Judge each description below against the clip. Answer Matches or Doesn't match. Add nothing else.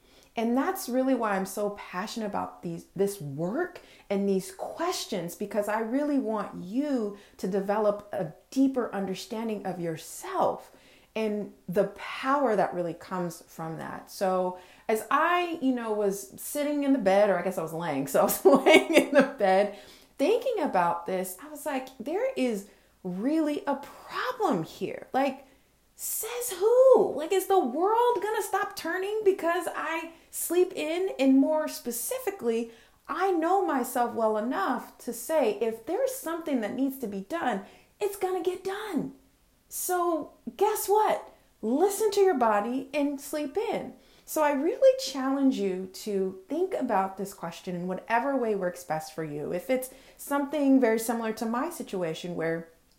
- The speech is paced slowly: Doesn't match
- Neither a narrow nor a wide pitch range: Doesn't match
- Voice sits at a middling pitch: Doesn't match